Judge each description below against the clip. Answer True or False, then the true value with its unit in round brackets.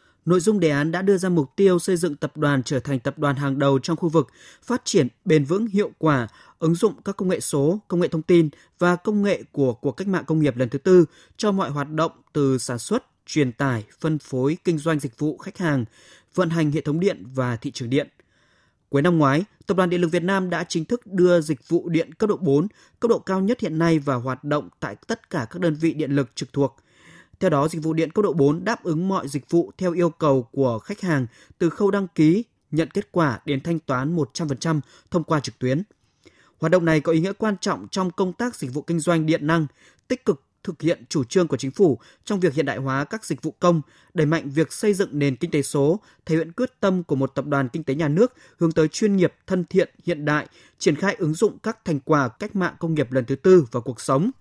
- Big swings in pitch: False (4.6 semitones)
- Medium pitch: True (160 Hz)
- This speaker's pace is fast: True (255 wpm)